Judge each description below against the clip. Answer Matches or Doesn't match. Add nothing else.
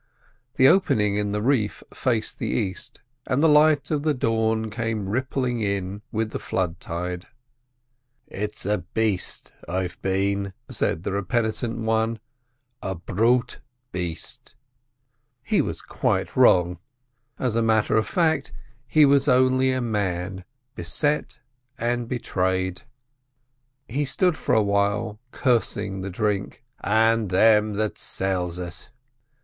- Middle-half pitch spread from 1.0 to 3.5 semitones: Doesn't match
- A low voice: Matches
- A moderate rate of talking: Doesn't match